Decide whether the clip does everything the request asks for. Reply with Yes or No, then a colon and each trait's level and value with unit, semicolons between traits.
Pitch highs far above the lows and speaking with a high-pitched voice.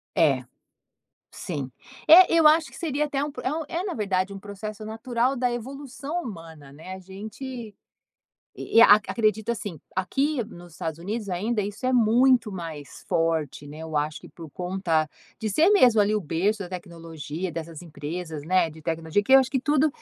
Yes: wide, 7.2 semitones; high, 200 Hz